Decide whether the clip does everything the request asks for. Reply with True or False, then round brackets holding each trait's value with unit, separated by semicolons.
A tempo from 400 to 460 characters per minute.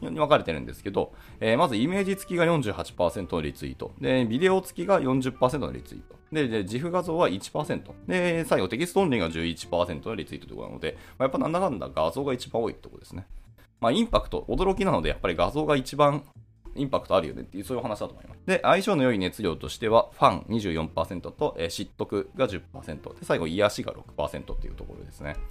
True (420 characters per minute)